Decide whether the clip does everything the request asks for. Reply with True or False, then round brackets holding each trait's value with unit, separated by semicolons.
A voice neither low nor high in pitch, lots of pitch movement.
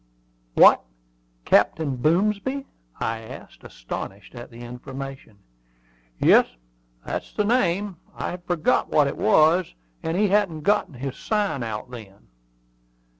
True (155 Hz; 8.5 semitones)